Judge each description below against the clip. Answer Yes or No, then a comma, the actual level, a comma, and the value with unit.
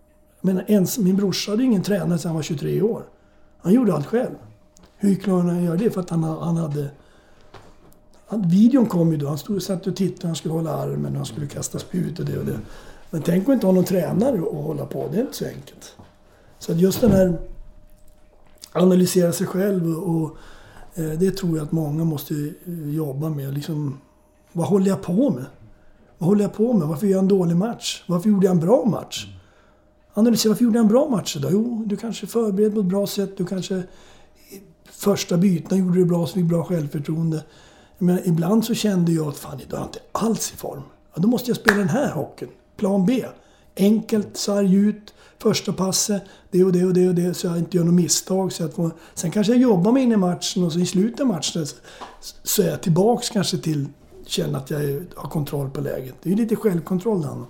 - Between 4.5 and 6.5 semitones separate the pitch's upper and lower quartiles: No, average, 4.1 semitones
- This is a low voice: No, medium, 180 Hz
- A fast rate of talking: Yes, fast, 220 wpm